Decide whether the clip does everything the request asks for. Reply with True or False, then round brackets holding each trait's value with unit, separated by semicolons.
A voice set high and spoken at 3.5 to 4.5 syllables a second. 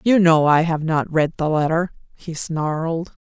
False (160 Hz; 4.3 syllables/s)